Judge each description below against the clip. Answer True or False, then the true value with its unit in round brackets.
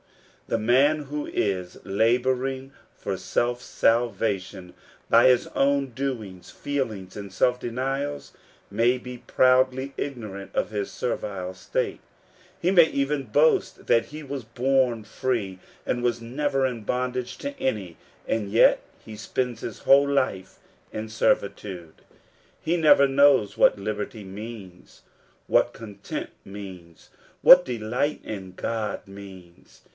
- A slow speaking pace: True (125 wpm)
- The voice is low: True (120 Hz)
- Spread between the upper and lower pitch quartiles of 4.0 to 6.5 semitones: True (4.9 semitones)